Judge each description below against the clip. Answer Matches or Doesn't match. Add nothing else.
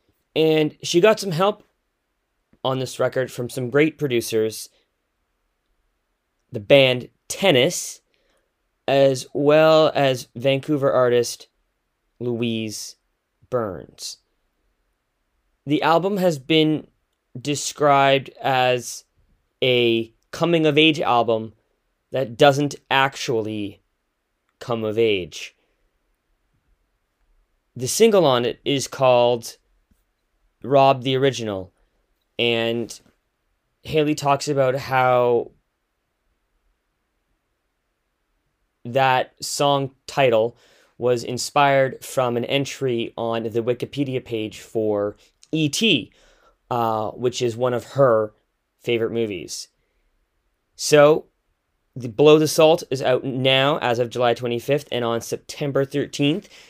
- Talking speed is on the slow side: Matches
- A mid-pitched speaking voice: Doesn't match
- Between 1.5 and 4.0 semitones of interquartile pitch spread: Matches